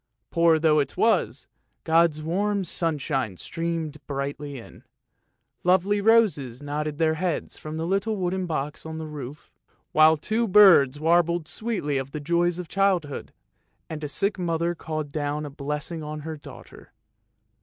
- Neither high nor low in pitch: Yes, medium, 160 Hz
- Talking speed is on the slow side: No, average, 155 wpm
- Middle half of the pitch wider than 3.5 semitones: No, average, 3.0 semitones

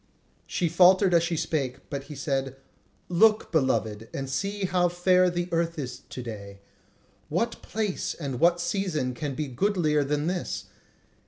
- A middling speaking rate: Yes, average, 155 wpm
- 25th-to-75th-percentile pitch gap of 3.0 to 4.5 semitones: No, average, 4.9 semitones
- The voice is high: No, medium, 165 Hz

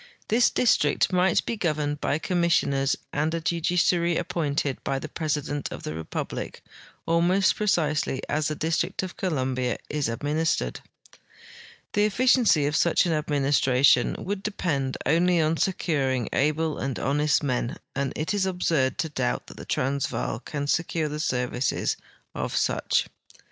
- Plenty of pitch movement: No, average, 3.9 semitones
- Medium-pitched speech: Yes, medium, 150 Hz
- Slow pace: No, average, 145 wpm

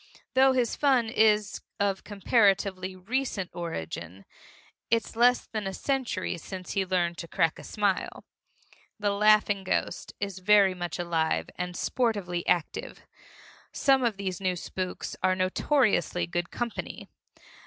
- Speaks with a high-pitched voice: Yes, high, 195 Hz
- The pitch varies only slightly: No, average, 3.7 semitones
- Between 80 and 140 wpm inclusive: Yes, slow, 135 wpm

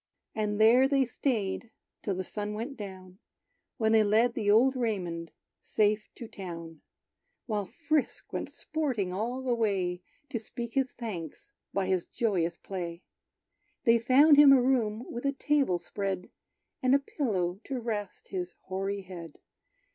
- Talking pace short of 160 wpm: Yes, average, 150 wpm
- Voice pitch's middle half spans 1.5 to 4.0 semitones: No, average, 4.9 semitones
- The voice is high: Yes, high, 215 Hz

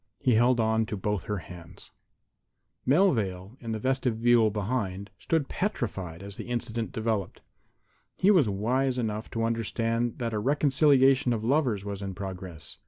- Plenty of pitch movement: No, average, 4.1 semitones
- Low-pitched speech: Yes, low, 115 Hz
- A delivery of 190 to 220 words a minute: No, average, 155 wpm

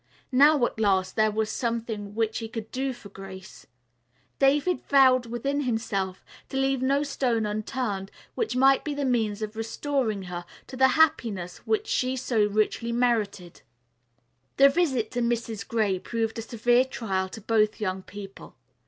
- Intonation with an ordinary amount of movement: Yes, average, 4.0 semitones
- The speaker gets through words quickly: No, average, 160 wpm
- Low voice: No, high, 230 Hz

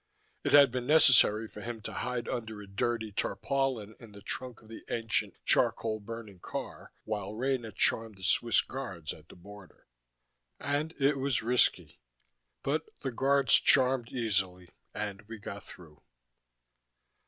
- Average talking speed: Yes, average, 150 wpm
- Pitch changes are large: No, average, 4.0 semitones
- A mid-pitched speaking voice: No, low, 115 Hz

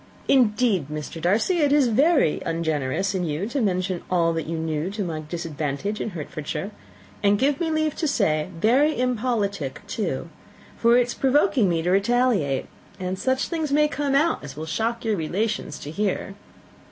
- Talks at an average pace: Yes, average, 175 wpm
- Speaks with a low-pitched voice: No, high, 200 Hz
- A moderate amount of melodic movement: No, wide, 7.5 semitones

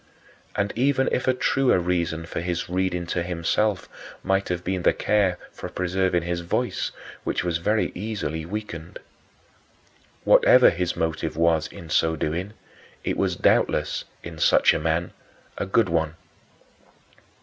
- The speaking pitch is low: Yes, very low, 90 Hz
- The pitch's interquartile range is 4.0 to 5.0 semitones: No, average, 2.7 semitones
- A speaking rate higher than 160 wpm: No, average, 140 wpm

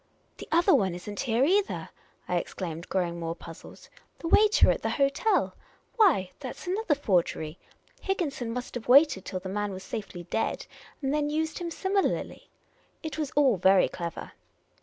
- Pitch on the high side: Yes, very high, 250 Hz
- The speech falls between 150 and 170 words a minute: No, average, 180 wpm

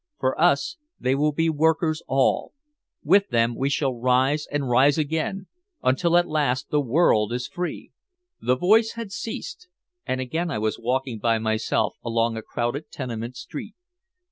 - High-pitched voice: No, medium, 140 Hz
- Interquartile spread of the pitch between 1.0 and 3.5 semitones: No, average, 5.2 semitones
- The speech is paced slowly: No, average, 160 wpm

